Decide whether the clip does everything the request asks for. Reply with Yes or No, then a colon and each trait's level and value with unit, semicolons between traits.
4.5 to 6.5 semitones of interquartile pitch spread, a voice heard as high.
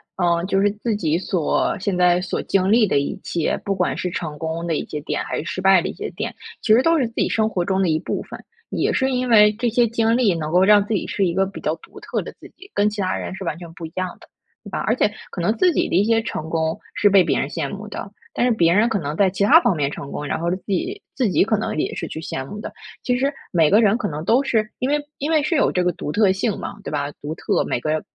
Yes: average, 4.9 semitones; high, 195 Hz